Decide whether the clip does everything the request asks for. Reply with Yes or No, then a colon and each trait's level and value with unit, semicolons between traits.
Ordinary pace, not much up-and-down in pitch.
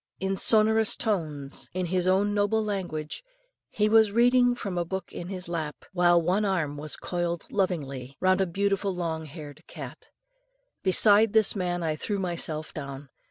No: average, 160 wpm; average, 4.3 semitones